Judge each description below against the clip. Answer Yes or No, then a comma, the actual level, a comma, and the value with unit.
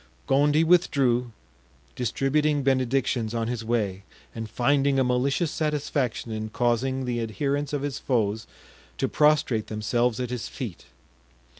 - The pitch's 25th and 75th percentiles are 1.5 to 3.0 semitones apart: No, average, 3.5 semitones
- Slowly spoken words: Yes, slow, 130 wpm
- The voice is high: No, low, 125 Hz